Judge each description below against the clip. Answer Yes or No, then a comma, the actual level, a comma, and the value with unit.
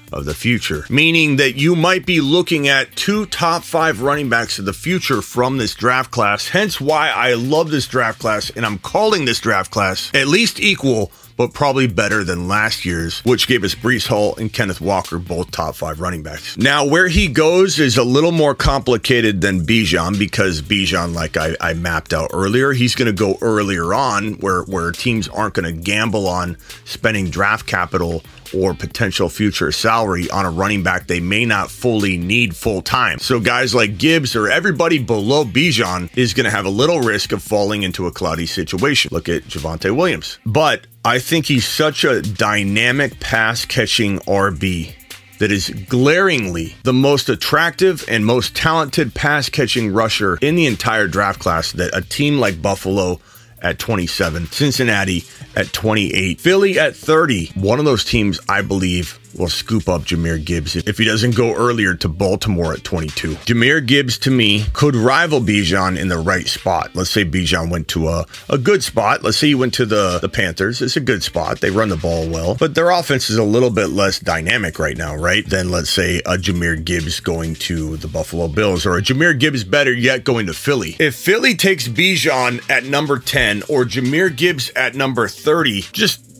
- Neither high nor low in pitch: No, low, 110 Hz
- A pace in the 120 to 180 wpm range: No, average, 190 wpm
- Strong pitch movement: Yes, wide, 6.0 semitones